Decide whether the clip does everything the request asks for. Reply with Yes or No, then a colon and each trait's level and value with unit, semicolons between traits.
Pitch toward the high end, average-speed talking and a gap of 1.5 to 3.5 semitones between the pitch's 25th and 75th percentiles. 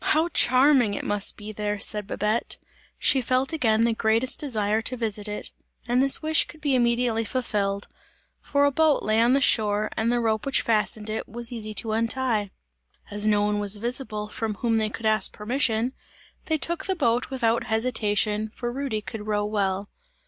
Yes: high, 225 Hz; average, 185 wpm; average, 3.2 semitones